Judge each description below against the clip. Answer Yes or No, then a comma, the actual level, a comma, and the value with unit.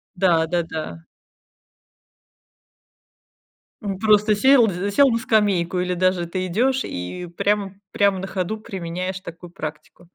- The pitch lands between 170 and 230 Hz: Yes, medium, 185 Hz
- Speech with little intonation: No, average, 3.2 semitones